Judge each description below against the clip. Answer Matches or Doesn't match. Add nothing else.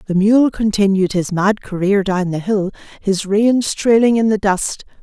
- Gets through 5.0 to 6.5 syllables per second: Doesn't match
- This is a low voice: Doesn't match